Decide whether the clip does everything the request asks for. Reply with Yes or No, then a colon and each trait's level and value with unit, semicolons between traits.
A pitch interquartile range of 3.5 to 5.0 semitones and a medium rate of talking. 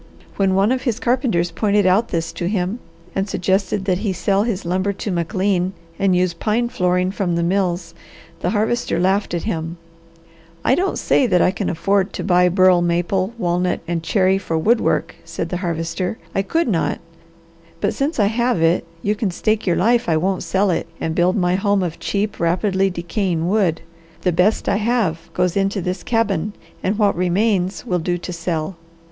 No: average, 2.9 semitones; average, 190 wpm